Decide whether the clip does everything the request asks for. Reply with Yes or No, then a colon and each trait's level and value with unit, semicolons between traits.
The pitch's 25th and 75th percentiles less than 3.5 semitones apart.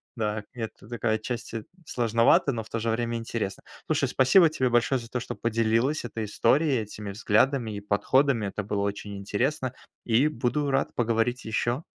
Yes: average, 3.0 semitones